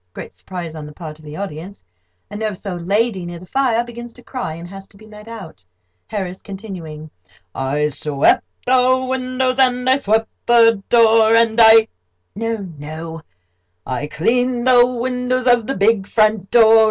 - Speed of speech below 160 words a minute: No, average, 165 wpm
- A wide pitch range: Yes, wide, 5.7 semitones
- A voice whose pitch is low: No, high, 220 Hz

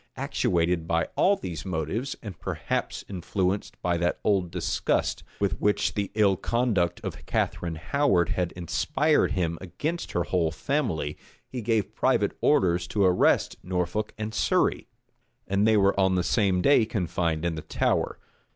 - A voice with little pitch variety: No, average, 3.5 semitones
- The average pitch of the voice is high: No, very low, 95 Hz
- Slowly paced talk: No, average, 150 wpm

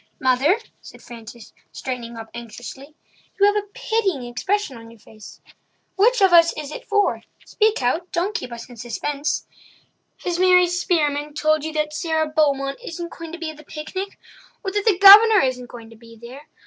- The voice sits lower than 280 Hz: No, very high, 305 Hz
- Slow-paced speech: No, average, 175 wpm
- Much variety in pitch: Yes, wide, 7.0 semitones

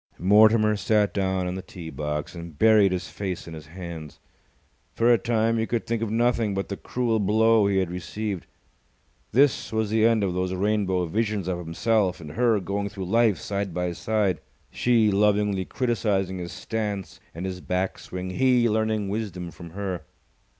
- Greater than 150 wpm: Yes, average, 180 wpm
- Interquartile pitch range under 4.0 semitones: Yes, average, 3.3 semitones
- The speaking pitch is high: No, low, 100 Hz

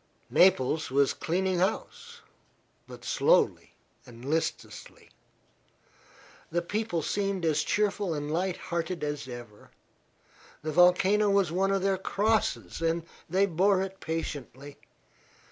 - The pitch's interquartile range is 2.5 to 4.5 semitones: Yes, average, 4.1 semitones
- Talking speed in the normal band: No, slow, 115 wpm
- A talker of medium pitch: Yes, medium, 180 Hz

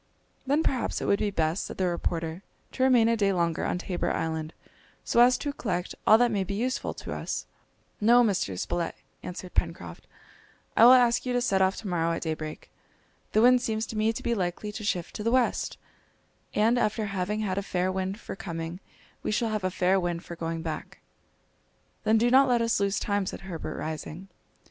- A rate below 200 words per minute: No, fast, 205 wpm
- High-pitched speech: Yes, high, 195 Hz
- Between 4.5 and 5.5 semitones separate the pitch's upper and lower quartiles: Yes, average, 4.8 semitones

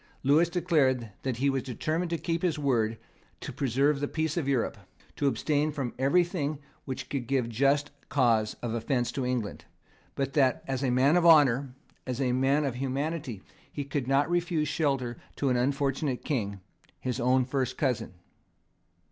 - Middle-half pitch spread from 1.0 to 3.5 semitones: Yes, average, 2.9 semitones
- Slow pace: No, average, 170 wpm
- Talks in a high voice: No, low, 135 Hz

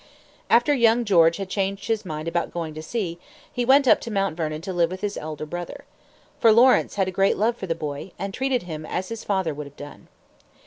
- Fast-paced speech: Yes, fast, 230 wpm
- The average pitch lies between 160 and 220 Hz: Yes, high, 190 Hz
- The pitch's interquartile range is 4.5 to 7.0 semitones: Yes, wide, 5.4 semitones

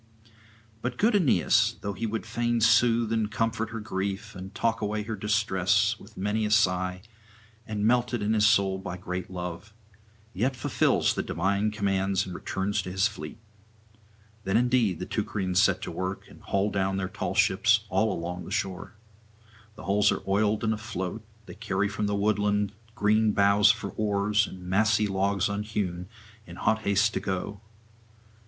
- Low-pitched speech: Yes, low, 105 Hz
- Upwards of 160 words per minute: Yes, average, 170 wpm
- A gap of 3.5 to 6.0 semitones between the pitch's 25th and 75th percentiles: No, narrow, 2.4 semitones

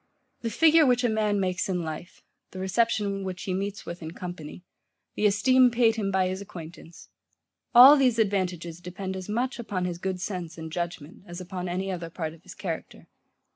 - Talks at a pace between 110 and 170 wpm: No, average, 190 wpm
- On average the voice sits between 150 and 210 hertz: Yes, high, 190 Hz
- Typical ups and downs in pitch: Yes, average, 3.5 semitones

